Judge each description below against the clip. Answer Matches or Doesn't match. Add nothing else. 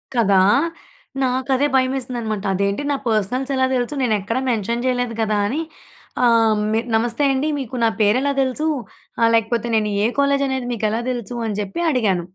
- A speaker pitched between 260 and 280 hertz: Doesn't match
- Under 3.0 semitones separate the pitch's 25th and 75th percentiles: Doesn't match